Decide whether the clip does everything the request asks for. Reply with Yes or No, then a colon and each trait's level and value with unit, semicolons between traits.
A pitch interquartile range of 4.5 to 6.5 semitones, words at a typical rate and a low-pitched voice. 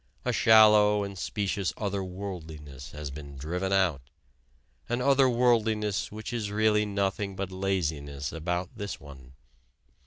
No: average, 4.9 semitones; slow, 130 wpm; very low, 95 Hz